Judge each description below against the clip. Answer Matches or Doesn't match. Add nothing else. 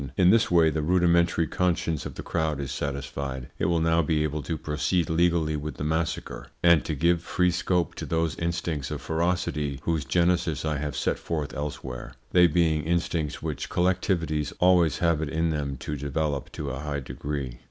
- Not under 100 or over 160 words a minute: Doesn't match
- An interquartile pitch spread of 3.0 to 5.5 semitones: Doesn't match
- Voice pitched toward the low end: Matches